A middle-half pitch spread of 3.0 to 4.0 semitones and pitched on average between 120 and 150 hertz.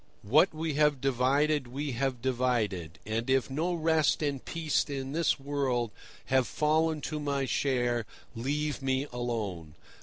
Yes: average, 3.6 semitones; low, 135 Hz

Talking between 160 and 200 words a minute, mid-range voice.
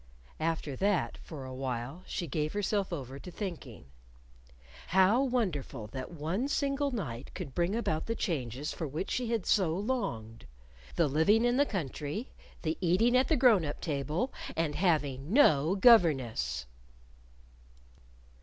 No: average, 145 wpm; medium, 165 Hz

